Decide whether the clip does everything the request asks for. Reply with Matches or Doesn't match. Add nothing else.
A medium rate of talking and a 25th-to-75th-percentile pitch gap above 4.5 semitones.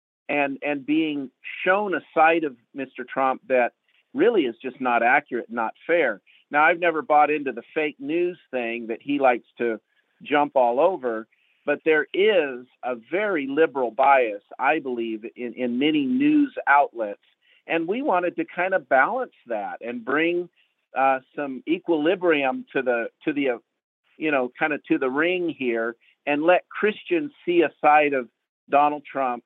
Matches